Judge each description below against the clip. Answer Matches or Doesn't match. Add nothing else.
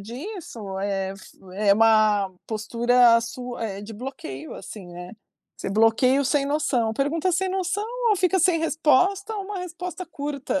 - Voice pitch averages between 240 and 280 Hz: Matches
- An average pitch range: Doesn't match